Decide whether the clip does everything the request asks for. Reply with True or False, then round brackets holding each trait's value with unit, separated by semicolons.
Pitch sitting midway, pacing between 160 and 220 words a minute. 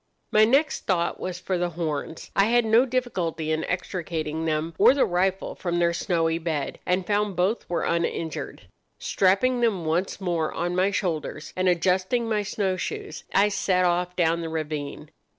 True (180 Hz; 170 wpm)